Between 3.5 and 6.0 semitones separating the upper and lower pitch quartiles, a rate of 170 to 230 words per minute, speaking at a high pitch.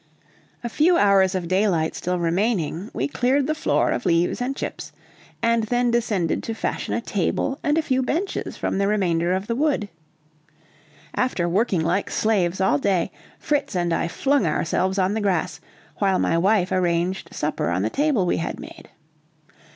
Yes: wide, 5.6 semitones; average, 175 wpm; high, 195 Hz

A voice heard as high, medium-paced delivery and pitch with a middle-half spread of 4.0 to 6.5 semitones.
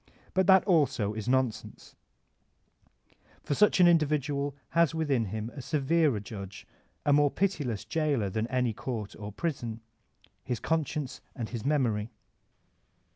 No: low, 135 Hz; average, 155 wpm; wide, 5.6 semitones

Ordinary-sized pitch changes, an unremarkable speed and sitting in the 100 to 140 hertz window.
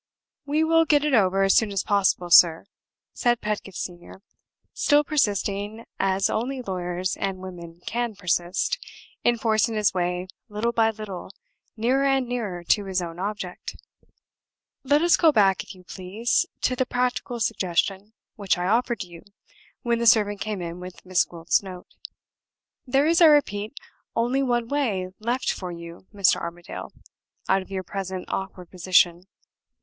No: average, 4.7 semitones; average, 160 wpm; high, 205 Hz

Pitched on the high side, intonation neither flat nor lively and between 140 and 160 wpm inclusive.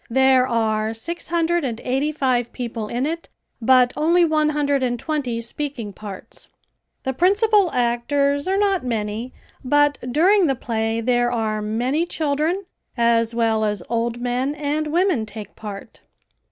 Yes: very high, 255 Hz; average, 4.8 semitones; average, 150 wpm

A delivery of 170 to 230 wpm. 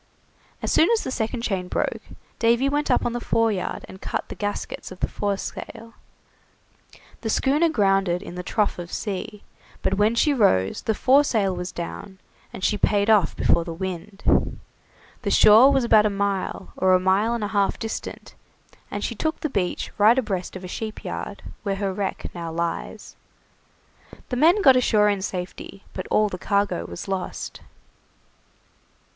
Yes: average, 175 wpm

